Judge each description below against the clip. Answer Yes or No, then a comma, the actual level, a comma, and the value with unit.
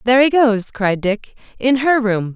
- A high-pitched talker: Yes, high, 230 Hz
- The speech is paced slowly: No, fast, 205 wpm